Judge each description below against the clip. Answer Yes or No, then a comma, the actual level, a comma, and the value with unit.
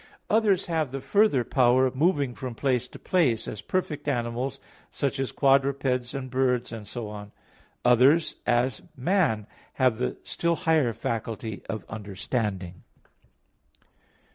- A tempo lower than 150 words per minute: Yes, slow, 135 wpm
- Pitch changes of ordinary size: Yes, average, 3.5 semitones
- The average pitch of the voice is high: No, low, 130 Hz